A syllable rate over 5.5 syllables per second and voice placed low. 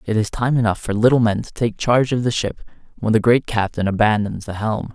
Yes: 5.7 syllables/s; low, 110 Hz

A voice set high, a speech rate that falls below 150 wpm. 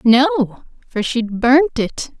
Yes: high, 245 Hz; slow, 135 wpm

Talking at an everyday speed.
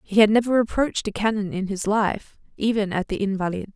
No: fast, 210 wpm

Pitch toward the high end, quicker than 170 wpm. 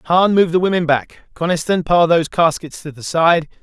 No: medium, 165 Hz; average, 200 wpm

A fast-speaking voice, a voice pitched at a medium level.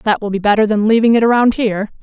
No: fast, 265 wpm; high, 215 Hz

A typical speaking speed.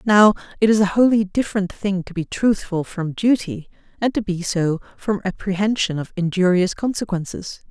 Yes: average, 165 wpm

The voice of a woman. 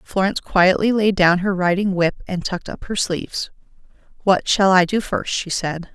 Yes: female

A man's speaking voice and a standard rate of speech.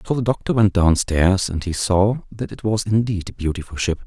No: male; fast, 220 wpm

